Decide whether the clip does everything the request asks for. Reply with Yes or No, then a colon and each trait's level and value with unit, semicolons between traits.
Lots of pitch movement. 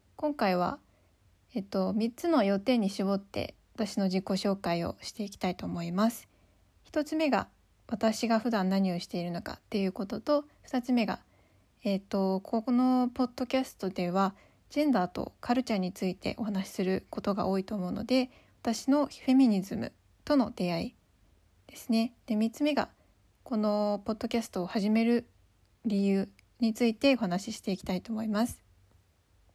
No: average, 4.0 semitones